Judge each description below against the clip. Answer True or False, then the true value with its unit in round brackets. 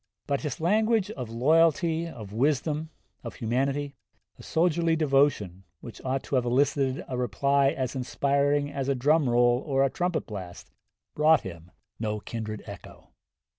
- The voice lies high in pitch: False (140 Hz)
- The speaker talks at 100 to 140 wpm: False (150 wpm)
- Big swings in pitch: False (4.2 semitones)